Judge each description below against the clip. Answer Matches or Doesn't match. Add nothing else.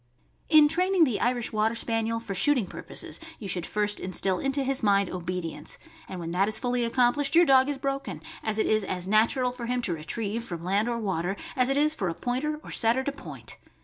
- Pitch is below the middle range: Doesn't match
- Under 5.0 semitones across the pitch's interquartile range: Doesn't match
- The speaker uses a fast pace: Matches